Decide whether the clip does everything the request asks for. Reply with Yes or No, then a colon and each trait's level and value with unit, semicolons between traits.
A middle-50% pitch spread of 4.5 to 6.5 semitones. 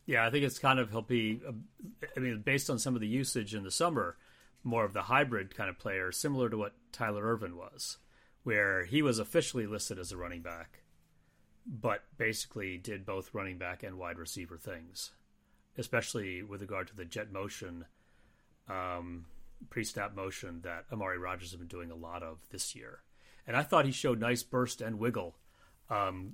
Yes: average, 5.0 semitones